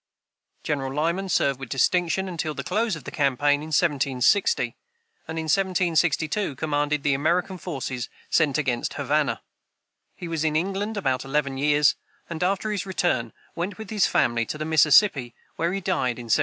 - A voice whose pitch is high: No, medium, 155 Hz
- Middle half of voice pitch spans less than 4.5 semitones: No, average, 4.8 semitones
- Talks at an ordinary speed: Yes, average, 170 wpm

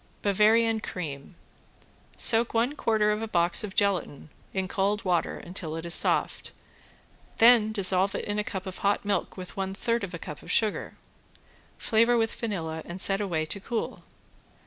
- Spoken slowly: No, average, 170 wpm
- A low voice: No, high, 200 Hz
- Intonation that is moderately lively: Yes, average, 3.4 semitones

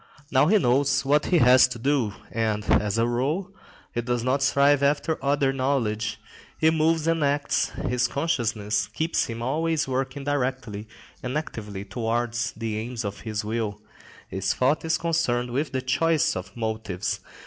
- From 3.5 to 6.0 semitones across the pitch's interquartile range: Yes, average, 4.3 semitones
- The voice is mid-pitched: No, low, 125 Hz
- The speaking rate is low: No, average, 160 wpm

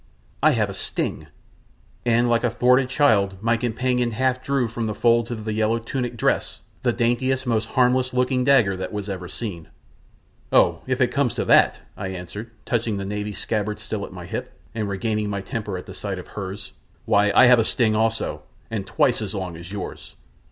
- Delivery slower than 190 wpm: No, average, 200 wpm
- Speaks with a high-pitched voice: No, low, 110 Hz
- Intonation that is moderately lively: Yes, average, 3.3 semitones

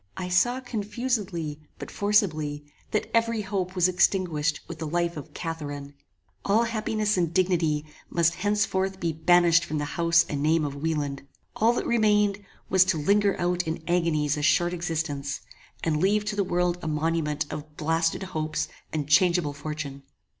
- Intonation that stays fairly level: No, average, 4.2 semitones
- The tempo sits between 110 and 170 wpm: Yes, average, 160 wpm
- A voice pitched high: No, medium, 170 Hz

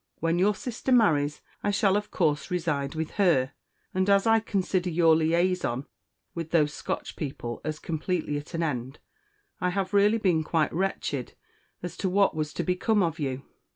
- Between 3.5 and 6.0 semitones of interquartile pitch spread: Yes, average, 4.3 semitones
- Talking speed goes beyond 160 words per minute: Yes, average, 175 wpm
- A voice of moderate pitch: Yes, medium, 170 Hz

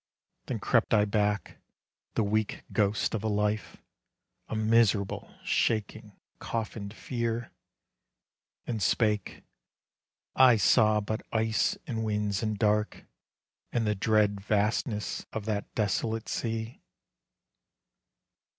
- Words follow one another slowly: Yes, slow, 105 wpm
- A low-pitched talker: Yes, low, 110 Hz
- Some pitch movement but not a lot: No, narrow, 1.4 semitones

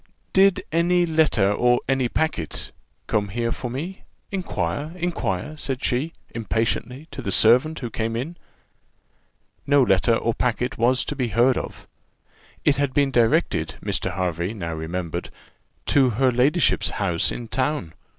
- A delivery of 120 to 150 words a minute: Yes, average, 140 wpm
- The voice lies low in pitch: Yes, low, 125 Hz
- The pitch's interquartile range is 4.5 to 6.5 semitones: Yes, average, 5.0 semitones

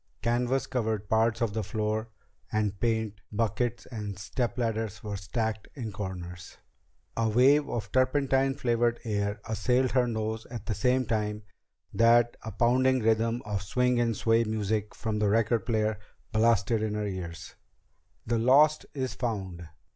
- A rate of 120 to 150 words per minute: Yes, average, 145 wpm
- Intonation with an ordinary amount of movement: No, narrow, 2.3 semitones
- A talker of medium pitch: No, low, 110 Hz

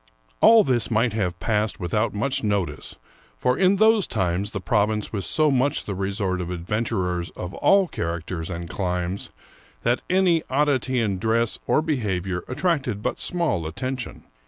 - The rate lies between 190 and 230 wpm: No, average, 160 wpm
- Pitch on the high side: No, low, 105 Hz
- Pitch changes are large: Yes, wide, 6.4 semitones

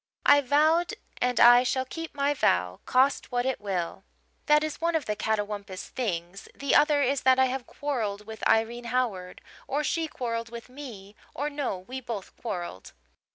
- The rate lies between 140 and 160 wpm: No, average, 175 wpm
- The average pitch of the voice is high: Yes, high, 245 Hz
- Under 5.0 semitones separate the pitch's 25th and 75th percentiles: No, average, 5.3 semitones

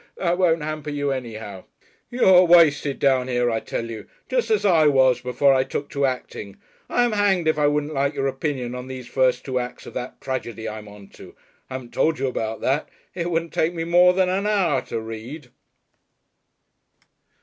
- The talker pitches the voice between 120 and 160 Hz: Yes, medium, 140 Hz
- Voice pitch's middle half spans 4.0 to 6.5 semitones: Yes, average, 5.1 semitones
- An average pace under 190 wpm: No, average, 195 wpm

